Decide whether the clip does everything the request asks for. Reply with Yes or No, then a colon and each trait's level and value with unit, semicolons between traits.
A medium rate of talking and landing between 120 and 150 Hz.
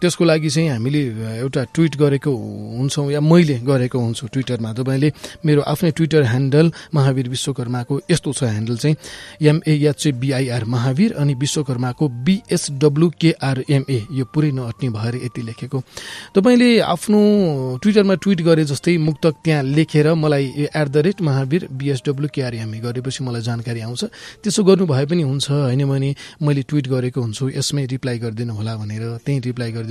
Yes: average, 155 wpm; medium, 140 Hz